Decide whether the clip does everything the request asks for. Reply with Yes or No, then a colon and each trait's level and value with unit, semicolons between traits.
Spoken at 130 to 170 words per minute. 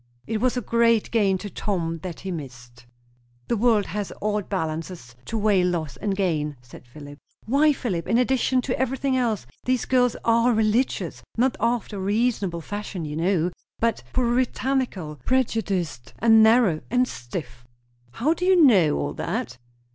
Yes: average, 160 wpm